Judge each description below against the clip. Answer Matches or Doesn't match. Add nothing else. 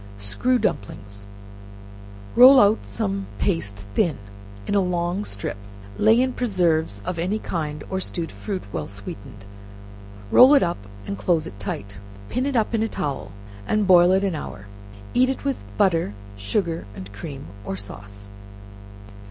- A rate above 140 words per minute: Matches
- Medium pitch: Matches